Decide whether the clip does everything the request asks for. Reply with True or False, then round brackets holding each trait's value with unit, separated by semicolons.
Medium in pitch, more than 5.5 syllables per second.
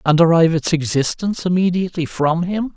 True (170 Hz; 6.0 syllables/s)